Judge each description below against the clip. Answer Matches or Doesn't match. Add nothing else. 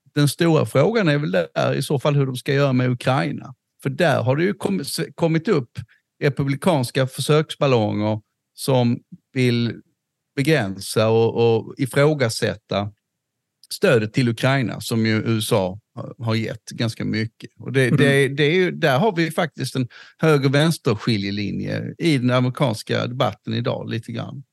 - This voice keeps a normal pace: Matches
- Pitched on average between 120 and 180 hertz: Matches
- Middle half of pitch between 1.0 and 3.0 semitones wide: Doesn't match